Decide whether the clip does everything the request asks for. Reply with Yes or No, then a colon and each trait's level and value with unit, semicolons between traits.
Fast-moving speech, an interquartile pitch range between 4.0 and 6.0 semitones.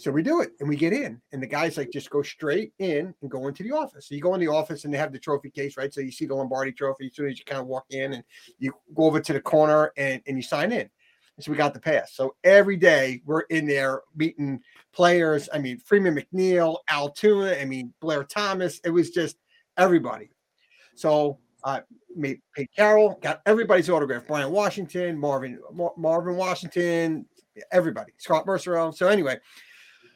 Yes: fast, 215 wpm; average, 4.4 semitones